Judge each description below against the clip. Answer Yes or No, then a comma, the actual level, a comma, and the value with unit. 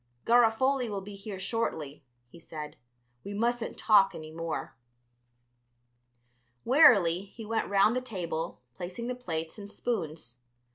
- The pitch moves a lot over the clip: Yes, wide, 5.8 semitones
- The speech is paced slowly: Yes, slow, 130 wpm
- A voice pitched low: No, high, 200 Hz